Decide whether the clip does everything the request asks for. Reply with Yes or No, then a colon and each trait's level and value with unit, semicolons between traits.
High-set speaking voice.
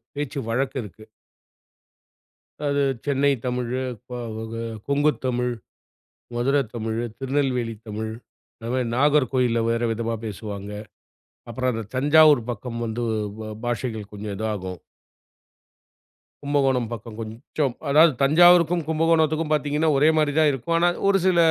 No: low, 130 Hz